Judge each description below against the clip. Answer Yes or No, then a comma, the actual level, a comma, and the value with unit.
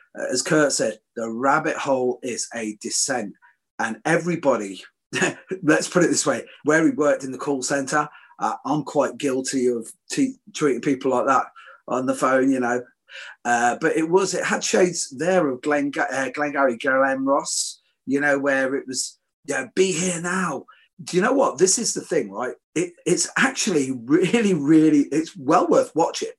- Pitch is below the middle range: No, medium, 145 Hz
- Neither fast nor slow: Yes, average, 185 wpm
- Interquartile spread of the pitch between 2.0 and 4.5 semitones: No, average, 5.2 semitones